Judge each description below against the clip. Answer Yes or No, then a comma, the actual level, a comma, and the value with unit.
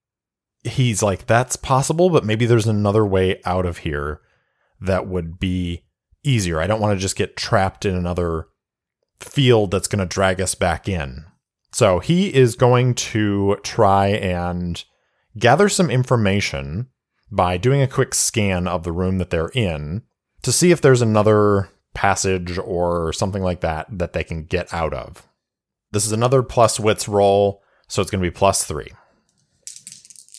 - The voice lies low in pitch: Yes, low, 100 Hz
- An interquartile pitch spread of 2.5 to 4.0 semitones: No, average, 4.6 semitones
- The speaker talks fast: No, average, 165 wpm